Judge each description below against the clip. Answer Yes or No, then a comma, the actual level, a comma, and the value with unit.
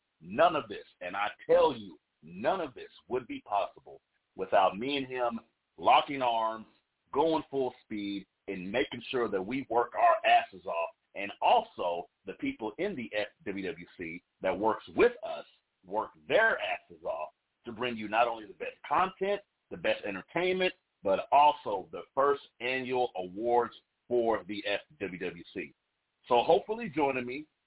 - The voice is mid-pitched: Yes, medium, 145 Hz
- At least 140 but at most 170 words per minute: Yes, average, 150 wpm